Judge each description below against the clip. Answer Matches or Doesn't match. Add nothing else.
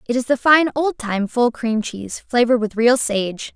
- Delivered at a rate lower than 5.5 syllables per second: Matches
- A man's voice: Doesn't match